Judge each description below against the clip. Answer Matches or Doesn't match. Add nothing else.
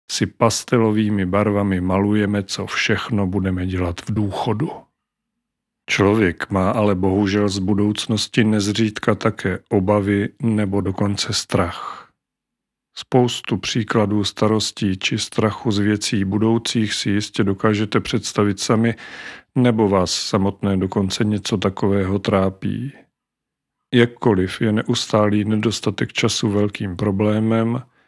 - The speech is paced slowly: Matches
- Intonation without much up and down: Matches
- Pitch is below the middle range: Matches